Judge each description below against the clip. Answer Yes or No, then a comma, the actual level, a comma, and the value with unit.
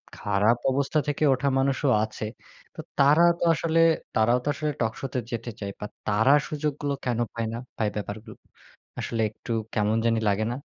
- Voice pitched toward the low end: Yes, low, 120 Hz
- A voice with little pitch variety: No, average, 4.4 semitones